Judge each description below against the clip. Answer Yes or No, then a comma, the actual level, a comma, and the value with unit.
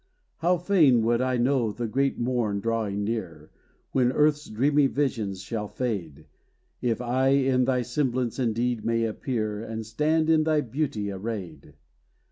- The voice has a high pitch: No, low, 120 Hz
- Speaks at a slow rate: No, average, 145 wpm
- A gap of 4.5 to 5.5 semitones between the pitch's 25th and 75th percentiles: No, average, 3.8 semitones